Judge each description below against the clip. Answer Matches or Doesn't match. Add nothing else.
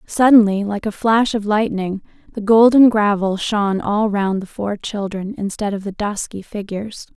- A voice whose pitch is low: Doesn't match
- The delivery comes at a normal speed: Matches